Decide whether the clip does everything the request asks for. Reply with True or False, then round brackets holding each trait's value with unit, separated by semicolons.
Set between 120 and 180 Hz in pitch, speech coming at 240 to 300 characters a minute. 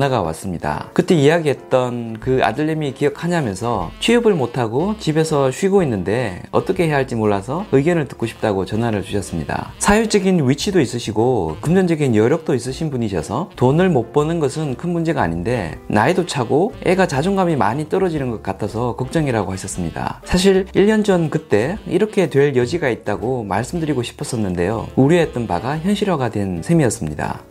False (135 Hz; 385 characters per minute)